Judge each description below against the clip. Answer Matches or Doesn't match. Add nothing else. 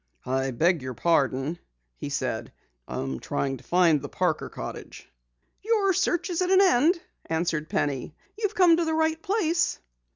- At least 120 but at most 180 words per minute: Matches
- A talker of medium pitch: Matches